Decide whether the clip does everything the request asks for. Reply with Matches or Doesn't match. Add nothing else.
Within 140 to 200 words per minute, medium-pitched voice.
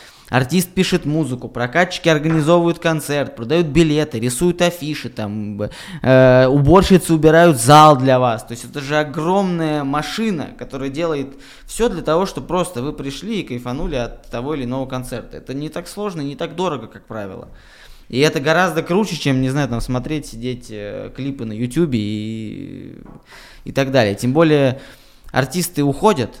Matches